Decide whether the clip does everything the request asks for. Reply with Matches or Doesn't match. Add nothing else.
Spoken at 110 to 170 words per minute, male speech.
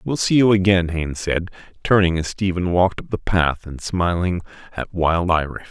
Doesn't match